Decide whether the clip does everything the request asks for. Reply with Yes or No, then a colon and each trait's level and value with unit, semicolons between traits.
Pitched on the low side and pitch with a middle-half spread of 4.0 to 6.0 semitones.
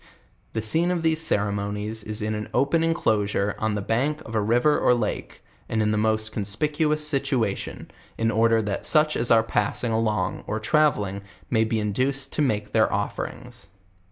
Yes: low, 110 Hz; average, 4.7 semitones